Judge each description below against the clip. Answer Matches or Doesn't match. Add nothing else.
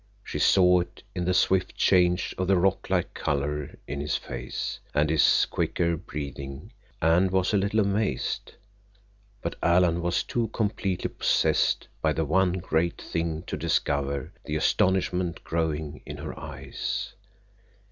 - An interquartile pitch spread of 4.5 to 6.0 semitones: Doesn't match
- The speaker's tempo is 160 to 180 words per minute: Doesn't match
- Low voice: Matches